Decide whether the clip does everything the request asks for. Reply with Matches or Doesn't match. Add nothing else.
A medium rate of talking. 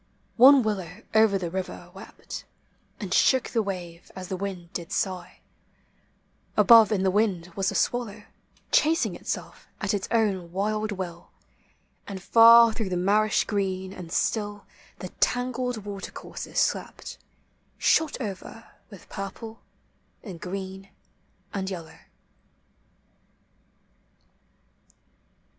Doesn't match